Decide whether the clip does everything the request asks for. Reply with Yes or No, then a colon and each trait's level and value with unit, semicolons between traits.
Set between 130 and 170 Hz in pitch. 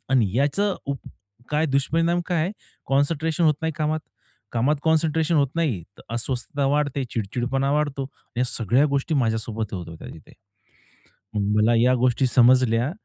Yes: low, 135 Hz